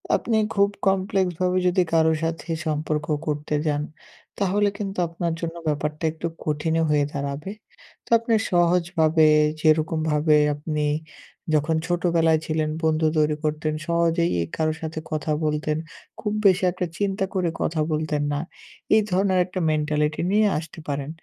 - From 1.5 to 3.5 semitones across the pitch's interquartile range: Yes, average, 2.9 semitones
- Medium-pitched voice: Yes, medium, 160 Hz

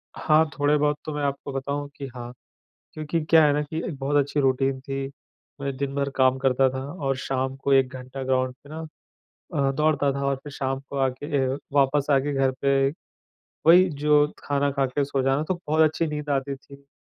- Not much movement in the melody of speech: Yes, narrow, 1.6 semitones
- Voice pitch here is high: No, medium, 140 Hz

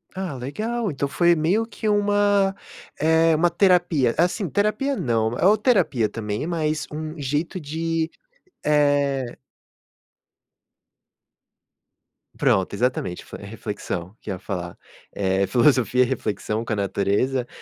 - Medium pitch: Yes, medium, 145 Hz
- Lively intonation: Yes, wide, 7.5 semitones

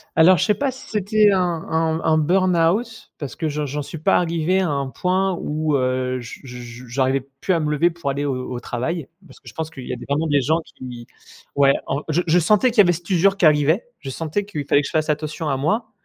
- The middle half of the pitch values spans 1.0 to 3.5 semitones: No, average, 4.5 semitones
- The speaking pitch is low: No, medium, 160 Hz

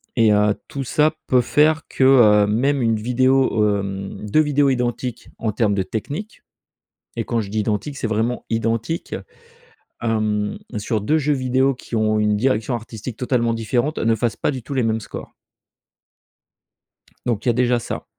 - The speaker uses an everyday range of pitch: Yes, average, 3.6 semitones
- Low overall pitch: Yes, low, 115 Hz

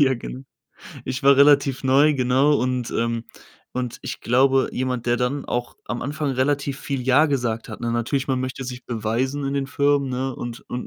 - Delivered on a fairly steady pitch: Yes, narrow, 2.1 semitones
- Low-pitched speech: Yes, low, 130 Hz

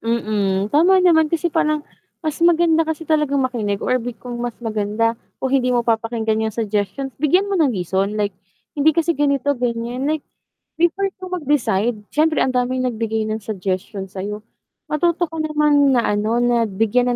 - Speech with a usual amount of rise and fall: No, wide, 5.8 semitones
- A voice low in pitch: No, high, 245 Hz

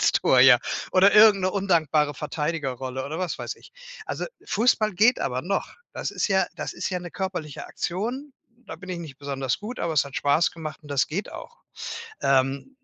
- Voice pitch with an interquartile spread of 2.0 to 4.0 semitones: No, wide, 5.8 semitones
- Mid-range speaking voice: Yes, medium, 165 Hz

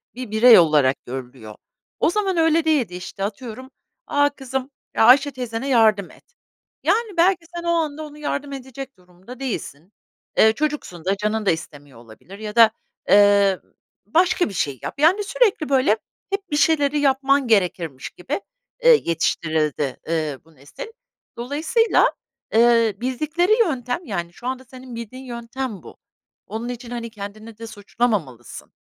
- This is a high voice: Yes, high, 240 Hz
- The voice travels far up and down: Yes, wide, 6.7 semitones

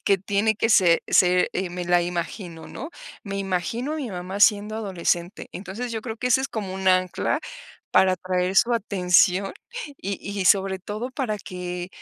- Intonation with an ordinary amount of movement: Yes, average, 3.0 semitones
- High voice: Yes, high, 195 Hz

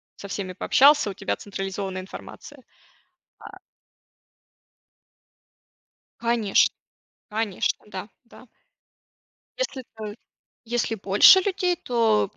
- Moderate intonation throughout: Yes, average, 3.6 semitones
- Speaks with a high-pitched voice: Yes, high, 215 Hz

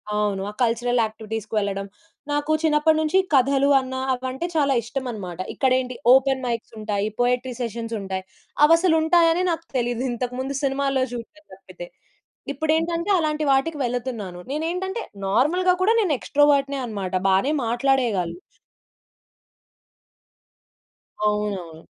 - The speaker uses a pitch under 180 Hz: No, very high, 260 Hz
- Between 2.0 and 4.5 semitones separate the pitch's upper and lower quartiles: No, wide, 5.5 semitones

